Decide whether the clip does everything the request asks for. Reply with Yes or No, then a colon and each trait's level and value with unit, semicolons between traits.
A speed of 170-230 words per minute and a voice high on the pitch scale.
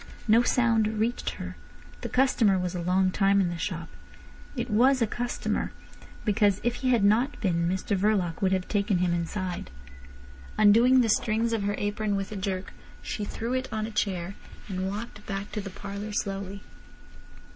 Yes: average, 180 wpm; high, 205 Hz